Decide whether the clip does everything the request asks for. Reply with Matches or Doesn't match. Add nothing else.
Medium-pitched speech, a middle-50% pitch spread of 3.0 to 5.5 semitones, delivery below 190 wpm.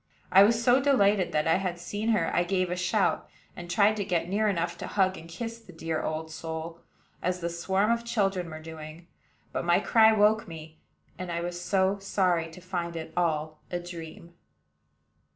Doesn't match